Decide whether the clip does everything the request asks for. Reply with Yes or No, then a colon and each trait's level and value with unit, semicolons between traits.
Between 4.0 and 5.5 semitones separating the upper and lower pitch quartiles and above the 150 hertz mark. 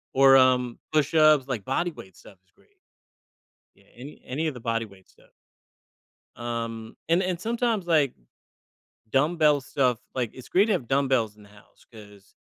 No: average, 5.2 semitones; low, 130 Hz